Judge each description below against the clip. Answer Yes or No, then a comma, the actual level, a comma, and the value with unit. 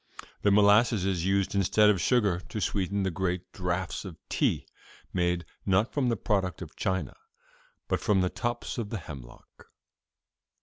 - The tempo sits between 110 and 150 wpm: No, average, 160 wpm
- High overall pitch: No, very low, 95 Hz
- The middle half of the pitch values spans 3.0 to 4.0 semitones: No, narrow, 2.6 semitones